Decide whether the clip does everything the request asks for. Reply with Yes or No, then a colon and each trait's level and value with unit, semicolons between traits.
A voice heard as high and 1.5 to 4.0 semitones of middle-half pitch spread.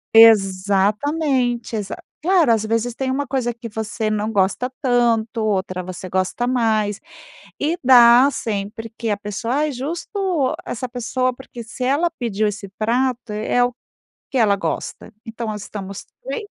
Yes: high, 230 Hz; average, 3.5 semitones